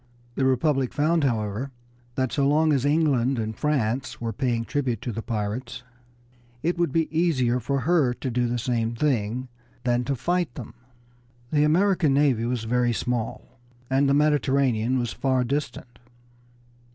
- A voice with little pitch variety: No, average, 3.5 semitones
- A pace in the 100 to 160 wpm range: Yes, average, 155 wpm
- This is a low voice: Yes, low, 130 Hz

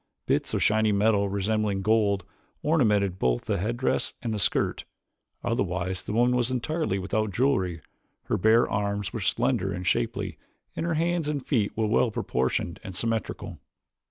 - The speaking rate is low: No, average, 155 wpm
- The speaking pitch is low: Yes, low, 105 Hz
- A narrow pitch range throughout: No, average, 3.7 semitones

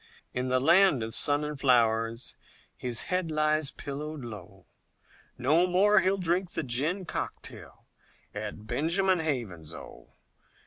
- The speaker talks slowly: Yes, slow, 130 wpm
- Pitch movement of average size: No, wide, 6.7 semitones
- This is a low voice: No, medium, 145 Hz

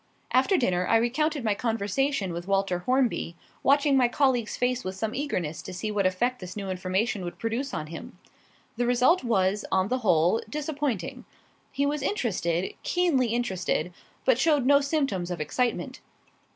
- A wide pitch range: Yes, wide, 6.5 semitones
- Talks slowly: No, average, 165 wpm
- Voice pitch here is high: Yes, high, 230 Hz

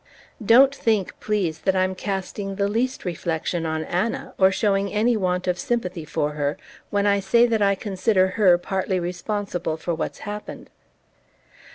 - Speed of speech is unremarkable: Yes, average, 160 wpm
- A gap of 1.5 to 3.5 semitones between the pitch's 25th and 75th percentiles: Yes, average, 2.9 semitones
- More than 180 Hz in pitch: Yes, high, 190 Hz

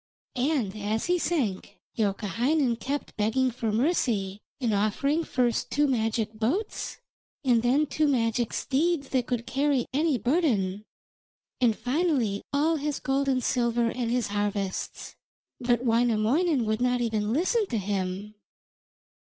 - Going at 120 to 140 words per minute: Yes, slow, 135 wpm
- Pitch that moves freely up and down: No, average, 4.6 semitones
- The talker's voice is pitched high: Yes, high, 245 Hz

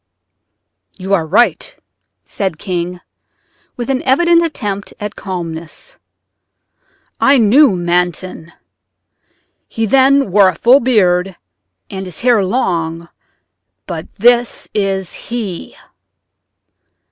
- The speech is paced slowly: Yes, slow, 100 wpm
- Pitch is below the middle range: No, high, 195 Hz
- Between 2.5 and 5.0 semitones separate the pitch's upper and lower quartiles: No, wide, 5.4 semitones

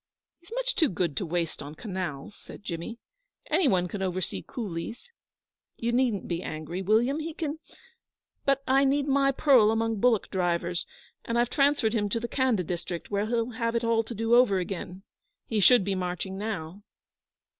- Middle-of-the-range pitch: No, high, 220 Hz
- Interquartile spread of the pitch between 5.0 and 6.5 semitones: Yes, wide, 5.5 semitones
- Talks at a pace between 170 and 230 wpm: Yes, average, 175 wpm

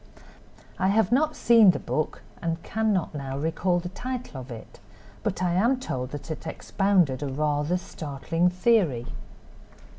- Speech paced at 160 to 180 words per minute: No, average, 150 wpm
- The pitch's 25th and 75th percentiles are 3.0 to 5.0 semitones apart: No, wide, 5.6 semitones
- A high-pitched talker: No, medium, 175 Hz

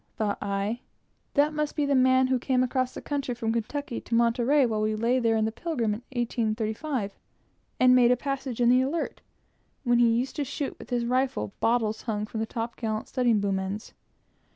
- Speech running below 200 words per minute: No, fast, 205 wpm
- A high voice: Yes, high, 240 Hz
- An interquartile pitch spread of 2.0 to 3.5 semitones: Yes, average, 2.8 semitones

